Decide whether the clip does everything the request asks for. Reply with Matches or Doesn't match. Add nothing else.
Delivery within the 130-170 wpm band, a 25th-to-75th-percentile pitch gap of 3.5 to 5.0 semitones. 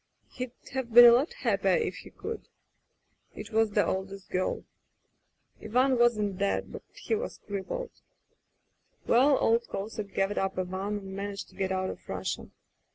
Matches